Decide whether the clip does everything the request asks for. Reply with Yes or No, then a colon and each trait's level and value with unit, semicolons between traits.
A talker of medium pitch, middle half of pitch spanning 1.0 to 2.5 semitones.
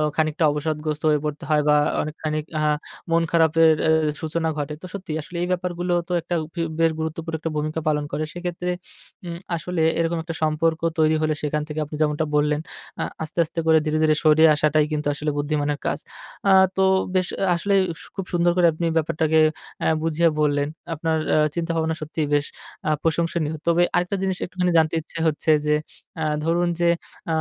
Yes: medium, 160 Hz; narrow, 1.9 semitones